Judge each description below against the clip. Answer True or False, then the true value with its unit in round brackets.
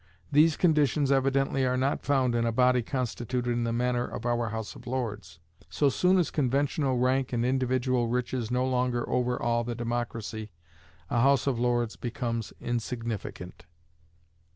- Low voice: True (125 Hz)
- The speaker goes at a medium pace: True (155 wpm)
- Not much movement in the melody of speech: True (2.0 semitones)